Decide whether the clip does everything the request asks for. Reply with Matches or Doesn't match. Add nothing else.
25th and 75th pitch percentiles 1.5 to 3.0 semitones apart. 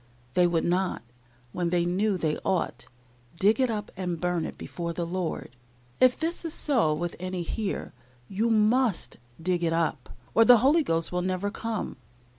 Doesn't match